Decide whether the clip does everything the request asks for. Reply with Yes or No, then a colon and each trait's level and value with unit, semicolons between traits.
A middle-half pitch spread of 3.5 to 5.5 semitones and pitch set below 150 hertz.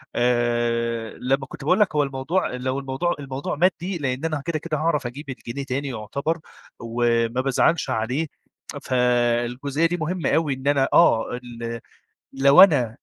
Yes: average, 4.1 semitones; low, 135 Hz